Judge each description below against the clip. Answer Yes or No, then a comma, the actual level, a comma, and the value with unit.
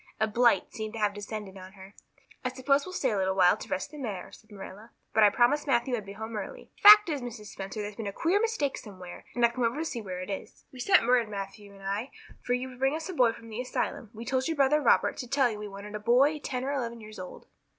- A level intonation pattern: No, average, 4.4 semitones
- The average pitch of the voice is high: Yes, high, 230 Hz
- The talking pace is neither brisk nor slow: No, fast, 275 wpm